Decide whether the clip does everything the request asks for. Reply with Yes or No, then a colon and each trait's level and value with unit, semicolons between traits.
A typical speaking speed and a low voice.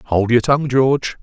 Yes: average, 195 wpm; low, 125 Hz